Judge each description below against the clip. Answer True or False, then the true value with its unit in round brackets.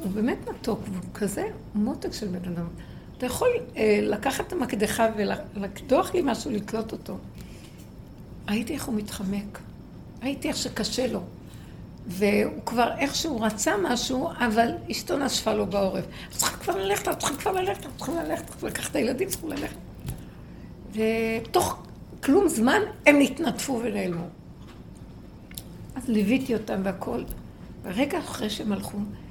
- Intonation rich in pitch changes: False (4.4 semitones)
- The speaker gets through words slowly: False (135 wpm)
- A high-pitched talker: True (225 Hz)